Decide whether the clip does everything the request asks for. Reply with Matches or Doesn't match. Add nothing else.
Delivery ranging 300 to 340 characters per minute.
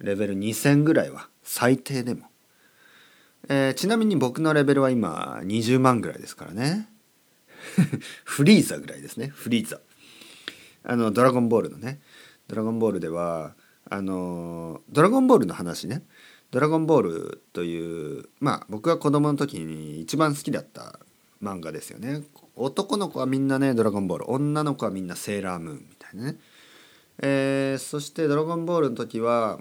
Matches